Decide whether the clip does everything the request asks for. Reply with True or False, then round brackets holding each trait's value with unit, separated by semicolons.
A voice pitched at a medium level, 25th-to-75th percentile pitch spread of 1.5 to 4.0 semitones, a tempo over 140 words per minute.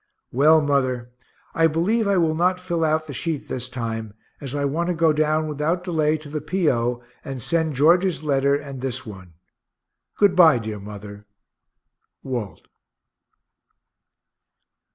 False (150 Hz; 4.6 semitones; 150 wpm)